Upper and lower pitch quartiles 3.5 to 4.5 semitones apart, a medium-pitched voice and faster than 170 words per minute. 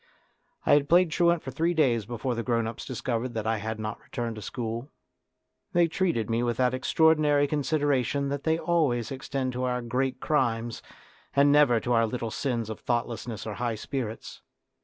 No: average, 3.9 semitones; low, 125 Hz; average, 180 wpm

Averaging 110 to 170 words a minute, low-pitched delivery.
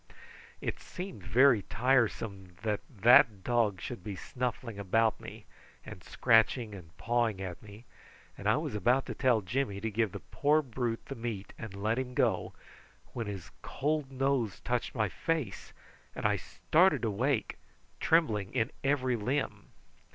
Yes: average, 150 wpm; low, 115 Hz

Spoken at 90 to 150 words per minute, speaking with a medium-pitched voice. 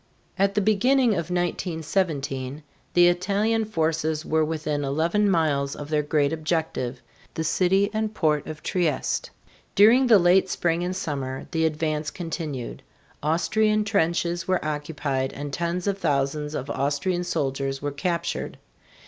Yes: average, 140 wpm; medium, 160 Hz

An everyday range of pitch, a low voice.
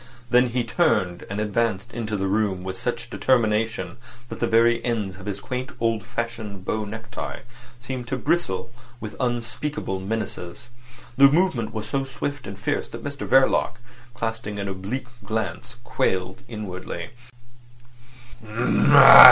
Yes: average, 3.3 semitones; low, 115 Hz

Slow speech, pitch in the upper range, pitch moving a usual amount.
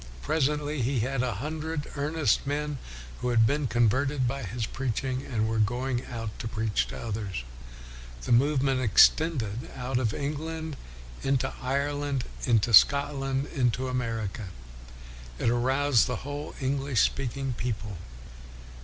No: slow, 130 wpm; low, 130 Hz; average, 3.5 semitones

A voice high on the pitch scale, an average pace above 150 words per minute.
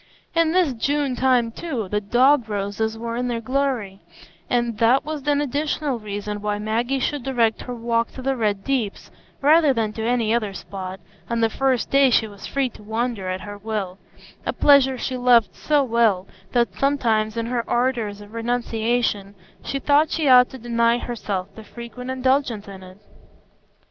Yes: high, 235 Hz; average, 175 wpm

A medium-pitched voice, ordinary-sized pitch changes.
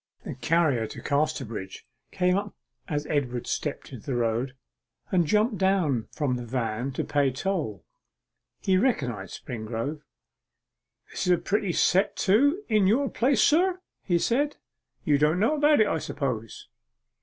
No: medium, 155 Hz; wide, 8.2 semitones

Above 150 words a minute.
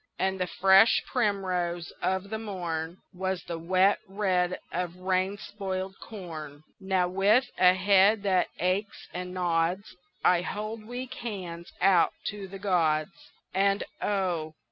No: slow, 135 wpm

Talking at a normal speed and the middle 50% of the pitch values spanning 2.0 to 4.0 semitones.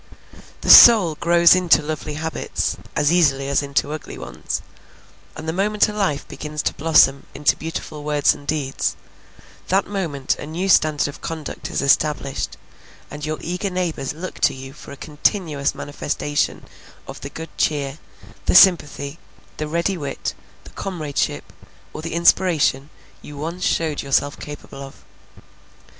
Yes: average, 150 wpm; average, 3.1 semitones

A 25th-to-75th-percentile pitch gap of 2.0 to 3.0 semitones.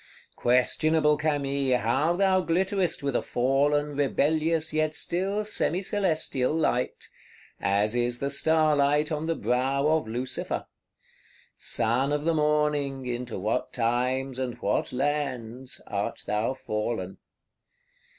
No: average, 3.8 semitones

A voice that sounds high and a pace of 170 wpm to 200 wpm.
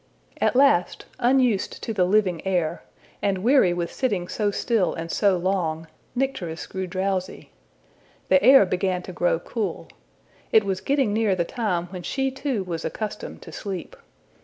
No: high, 195 Hz; average, 160 wpm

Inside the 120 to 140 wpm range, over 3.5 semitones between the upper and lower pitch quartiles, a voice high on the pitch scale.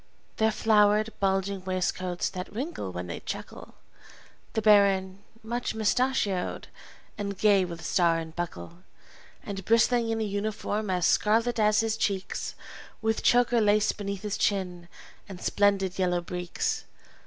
No: slow, 135 wpm; average, 3.0 semitones; high, 200 Hz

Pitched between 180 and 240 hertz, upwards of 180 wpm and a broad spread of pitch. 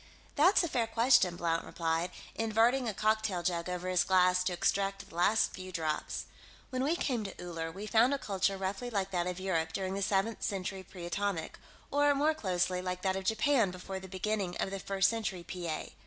No: high, 190 Hz; fast, 205 wpm; average, 3.5 semitones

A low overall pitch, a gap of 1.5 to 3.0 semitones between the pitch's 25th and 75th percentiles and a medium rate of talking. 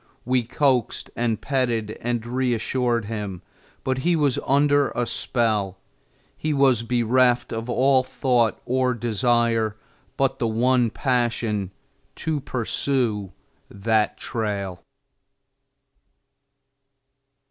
No: low, 120 Hz; average, 2.7 semitones; slow, 100 wpm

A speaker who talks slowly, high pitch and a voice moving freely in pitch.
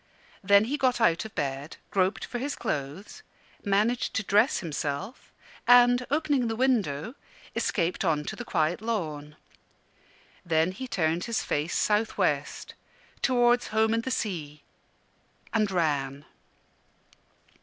Yes: slow, 130 wpm; high, 200 Hz; wide, 7.3 semitones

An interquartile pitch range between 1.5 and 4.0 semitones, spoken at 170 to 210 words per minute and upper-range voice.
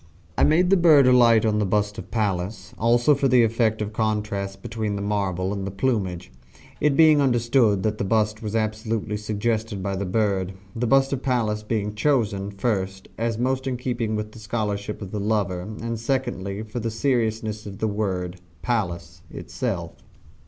No: average, 2.8 semitones; average, 180 wpm; low, 110 Hz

